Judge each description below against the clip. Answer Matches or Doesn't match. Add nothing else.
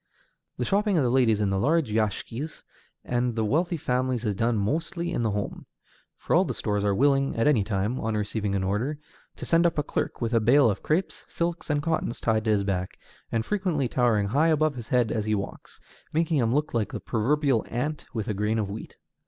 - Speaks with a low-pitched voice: Matches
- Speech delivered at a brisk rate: Matches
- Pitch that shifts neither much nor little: Doesn't match